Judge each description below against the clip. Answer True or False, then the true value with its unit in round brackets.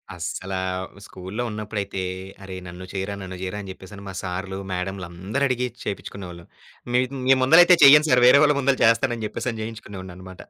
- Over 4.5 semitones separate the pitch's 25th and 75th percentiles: True (5.0 semitones)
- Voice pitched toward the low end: True (100 Hz)